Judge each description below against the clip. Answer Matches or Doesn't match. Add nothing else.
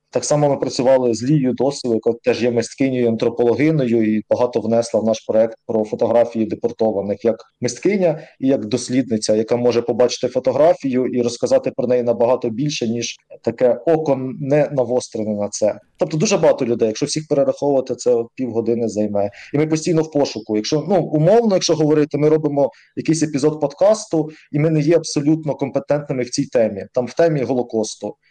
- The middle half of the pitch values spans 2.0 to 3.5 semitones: Doesn't match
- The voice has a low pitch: Matches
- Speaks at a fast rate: Matches